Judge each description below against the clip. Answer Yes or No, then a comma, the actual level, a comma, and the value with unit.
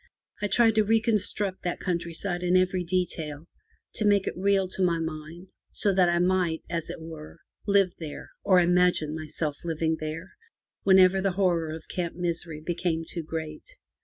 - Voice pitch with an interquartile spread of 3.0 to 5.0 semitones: No, narrow, 2.6 semitones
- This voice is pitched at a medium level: Yes, medium, 175 Hz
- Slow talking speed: No, average, 165 wpm